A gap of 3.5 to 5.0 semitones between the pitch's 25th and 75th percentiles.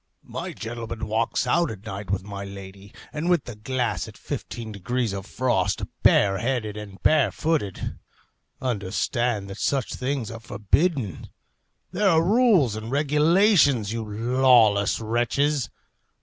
No: wide, 5.5 semitones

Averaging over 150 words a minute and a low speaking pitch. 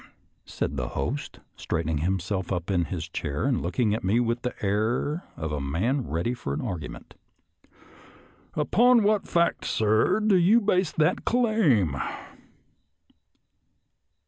No: average, 145 wpm; low, 110 Hz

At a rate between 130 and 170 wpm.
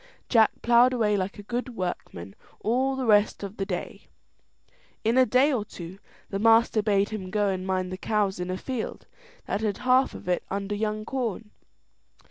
No: average, 185 wpm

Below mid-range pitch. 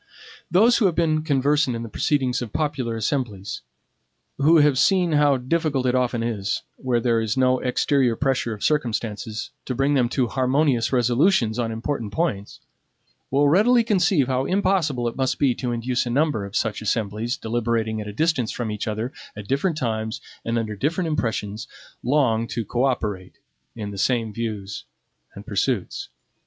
Yes: low, 125 Hz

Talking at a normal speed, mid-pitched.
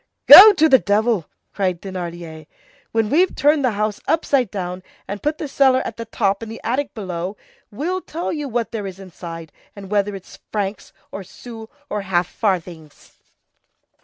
No: average, 170 wpm; high, 210 Hz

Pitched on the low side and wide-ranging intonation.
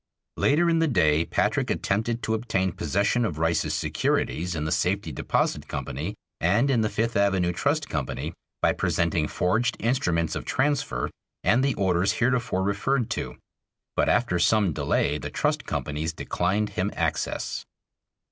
Yes: low, 100 Hz; wide, 5.9 semitones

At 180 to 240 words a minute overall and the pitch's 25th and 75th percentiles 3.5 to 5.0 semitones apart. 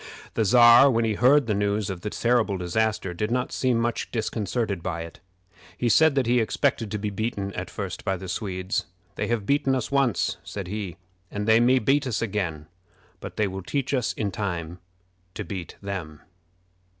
Yes: average, 190 wpm; average, 3.8 semitones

